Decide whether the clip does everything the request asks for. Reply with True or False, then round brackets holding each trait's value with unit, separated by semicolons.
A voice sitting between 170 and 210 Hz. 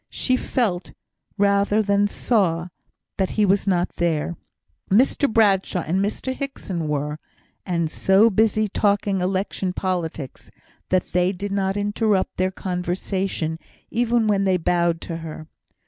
True (190 Hz)